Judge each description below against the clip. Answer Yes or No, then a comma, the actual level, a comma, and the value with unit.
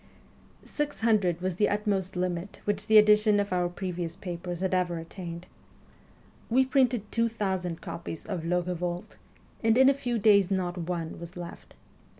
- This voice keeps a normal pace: Yes, average, 160 wpm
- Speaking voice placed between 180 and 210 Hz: Yes, medium, 185 Hz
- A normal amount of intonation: Yes, average, 3.3 semitones